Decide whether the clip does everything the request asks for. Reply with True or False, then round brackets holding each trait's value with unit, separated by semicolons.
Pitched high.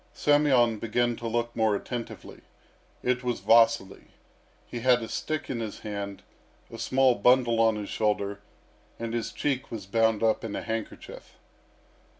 False (115 Hz)